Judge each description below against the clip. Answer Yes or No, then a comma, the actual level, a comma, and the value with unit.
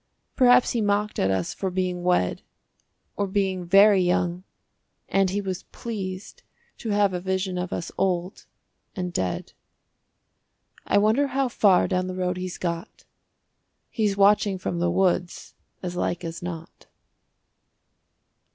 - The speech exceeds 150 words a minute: No, average, 140 wpm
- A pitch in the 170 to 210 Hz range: Yes, medium, 185 Hz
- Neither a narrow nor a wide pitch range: No, narrow, 2.3 semitones